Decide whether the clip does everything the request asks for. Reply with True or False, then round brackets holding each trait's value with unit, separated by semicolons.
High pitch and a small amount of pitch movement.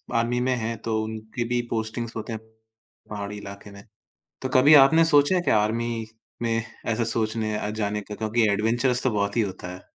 False (110 Hz; 2.2 semitones)